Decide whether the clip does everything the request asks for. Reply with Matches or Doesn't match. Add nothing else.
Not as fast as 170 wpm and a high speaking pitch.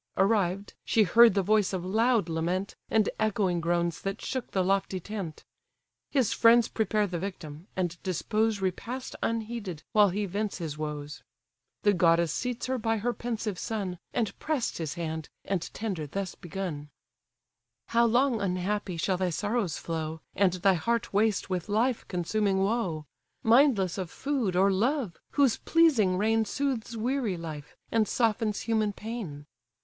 Matches